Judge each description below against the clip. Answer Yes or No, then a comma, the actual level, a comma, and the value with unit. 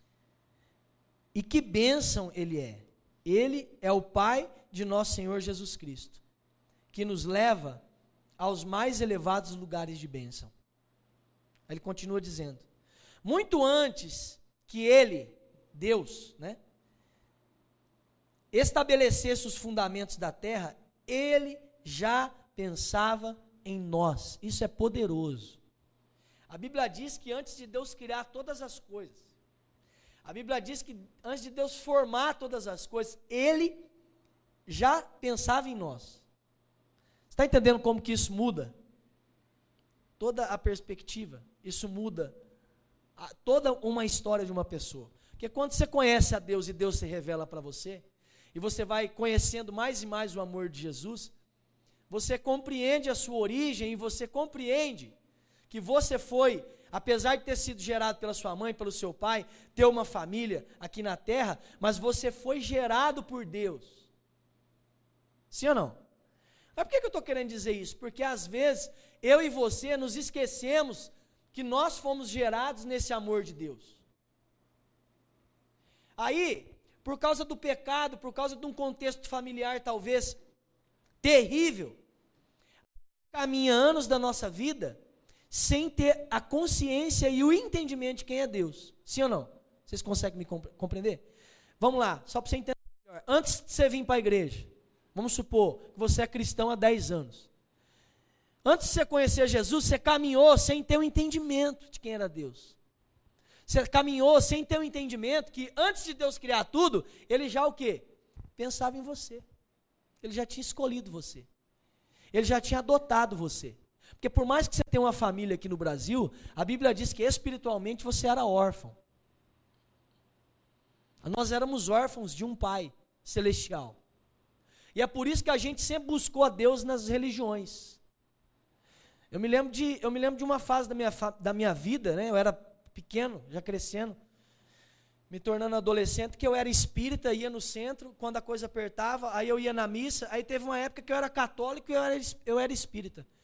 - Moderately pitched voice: No, high, 230 Hz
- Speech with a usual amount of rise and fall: No, wide, 5.7 semitones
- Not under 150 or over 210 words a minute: Yes, average, 155 wpm